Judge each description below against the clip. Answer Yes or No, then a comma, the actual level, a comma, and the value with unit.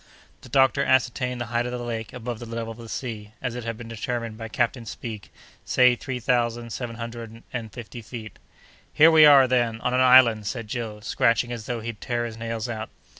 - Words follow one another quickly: Yes, fast, 215 wpm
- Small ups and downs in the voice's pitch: Yes, narrow, 1.6 semitones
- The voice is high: No, low, 120 Hz